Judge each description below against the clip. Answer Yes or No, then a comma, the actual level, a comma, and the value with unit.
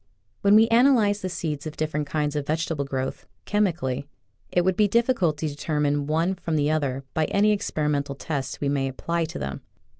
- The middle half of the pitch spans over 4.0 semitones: Yes, average, 4.6 semitones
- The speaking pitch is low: No, medium, 155 Hz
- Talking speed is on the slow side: No, average, 185 wpm